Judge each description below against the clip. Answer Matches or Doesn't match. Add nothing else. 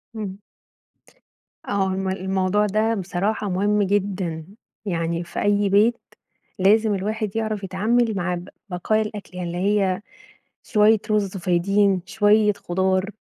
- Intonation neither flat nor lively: Doesn't match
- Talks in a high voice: Matches